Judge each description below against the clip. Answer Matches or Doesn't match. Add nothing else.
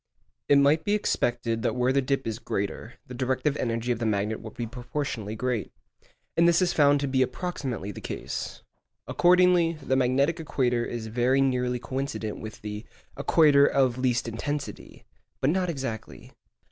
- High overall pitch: Doesn't match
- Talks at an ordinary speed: Matches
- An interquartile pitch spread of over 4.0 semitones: Doesn't match